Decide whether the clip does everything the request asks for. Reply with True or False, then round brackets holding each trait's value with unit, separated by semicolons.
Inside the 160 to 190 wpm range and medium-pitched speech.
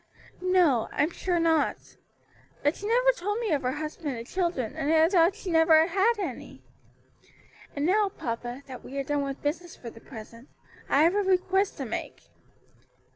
False (180 wpm; 320 Hz)